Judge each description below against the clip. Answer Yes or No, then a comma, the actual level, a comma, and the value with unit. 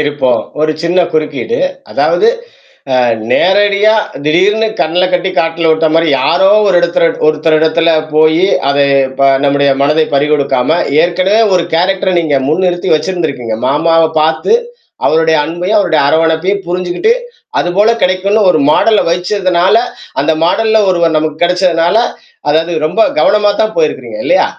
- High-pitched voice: No, medium, 170 Hz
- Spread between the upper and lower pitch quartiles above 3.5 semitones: No, average, 3.2 semitones